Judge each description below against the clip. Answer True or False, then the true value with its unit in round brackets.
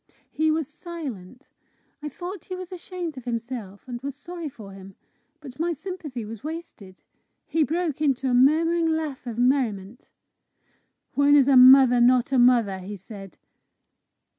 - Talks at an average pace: True (155 wpm)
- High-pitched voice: True (270 Hz)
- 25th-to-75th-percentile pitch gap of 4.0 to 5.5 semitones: True (5.0 semitones)